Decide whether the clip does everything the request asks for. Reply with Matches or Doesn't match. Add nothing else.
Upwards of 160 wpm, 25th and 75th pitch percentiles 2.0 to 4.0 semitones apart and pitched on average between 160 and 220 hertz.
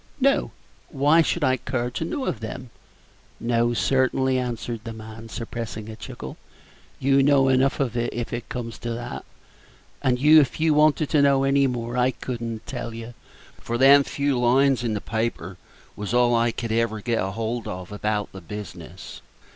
Doesn't match